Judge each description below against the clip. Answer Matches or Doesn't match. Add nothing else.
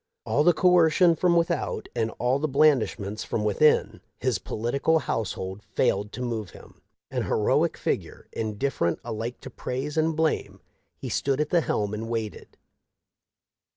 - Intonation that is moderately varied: Doesn't match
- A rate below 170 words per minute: Matches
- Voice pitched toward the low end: Matches